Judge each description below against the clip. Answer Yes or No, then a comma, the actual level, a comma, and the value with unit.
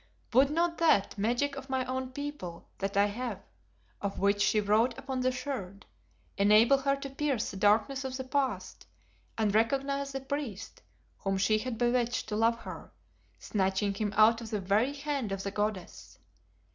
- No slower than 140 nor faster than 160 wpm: No, average, 170 wpm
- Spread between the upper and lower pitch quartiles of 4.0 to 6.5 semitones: Yes, average, 4.9 semitones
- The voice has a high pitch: Yes, high, 235 Hz